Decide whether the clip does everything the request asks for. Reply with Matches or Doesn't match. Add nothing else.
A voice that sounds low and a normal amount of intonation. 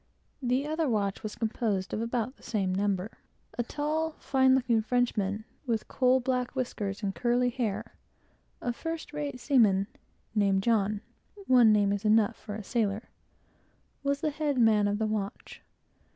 Doesn't match